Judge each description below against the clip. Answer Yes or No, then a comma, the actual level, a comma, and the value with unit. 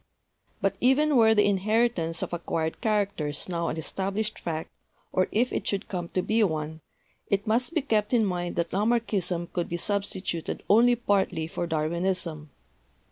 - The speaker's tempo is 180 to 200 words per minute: No, average, 165 wpm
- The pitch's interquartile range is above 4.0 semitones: Yes, average, 4.5 semitones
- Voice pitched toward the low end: No, high, 190 Hz